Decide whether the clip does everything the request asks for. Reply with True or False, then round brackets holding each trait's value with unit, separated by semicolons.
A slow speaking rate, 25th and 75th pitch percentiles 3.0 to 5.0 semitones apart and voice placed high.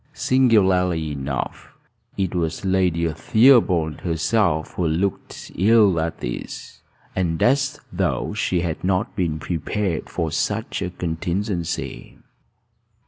False (110 wpm; 3.5 semitones; 90 Hz)